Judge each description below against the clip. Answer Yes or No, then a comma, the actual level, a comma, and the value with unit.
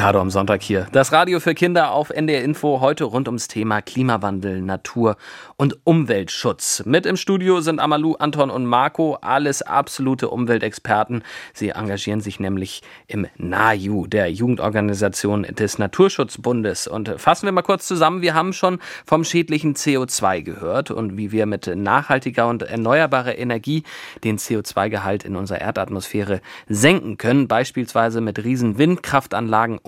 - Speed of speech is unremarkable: Yes, average, 145 wpm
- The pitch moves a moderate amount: No, wide, 6.2 semitones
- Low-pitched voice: Yes, low, 115 Hz